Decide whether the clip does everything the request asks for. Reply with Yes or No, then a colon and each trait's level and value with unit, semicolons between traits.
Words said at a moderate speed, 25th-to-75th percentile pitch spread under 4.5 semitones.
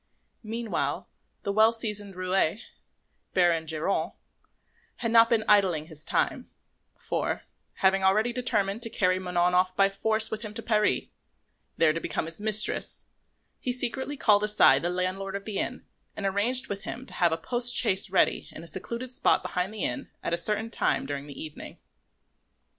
Yes: average, 170 wpm; average, 3.8 semitones